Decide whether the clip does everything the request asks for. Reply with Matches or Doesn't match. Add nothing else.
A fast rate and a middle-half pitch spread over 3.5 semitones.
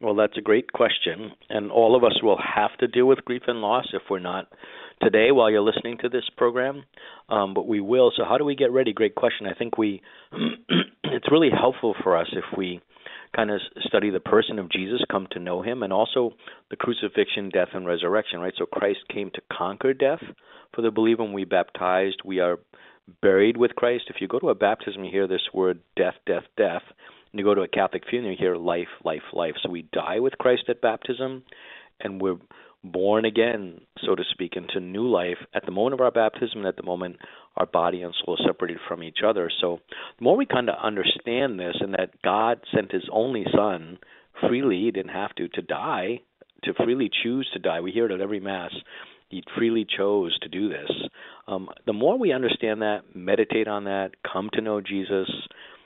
Matches